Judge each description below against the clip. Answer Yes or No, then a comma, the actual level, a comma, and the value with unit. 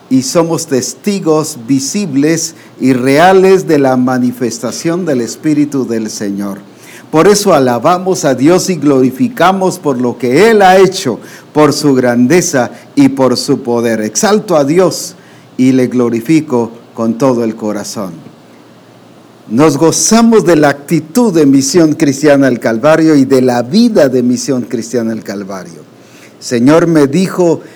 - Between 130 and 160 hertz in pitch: Yes, medium, 140 Hz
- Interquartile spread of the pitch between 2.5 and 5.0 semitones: No, wide, 5.6 semitones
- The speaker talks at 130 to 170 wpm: Yes, average, 140 wpm